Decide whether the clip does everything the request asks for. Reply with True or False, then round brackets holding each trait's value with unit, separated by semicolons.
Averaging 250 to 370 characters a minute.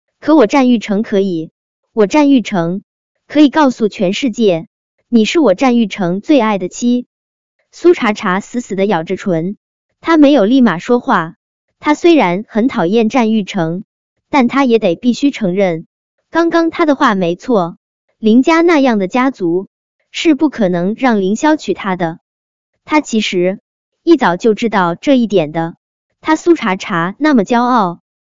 False (225 characters per minute)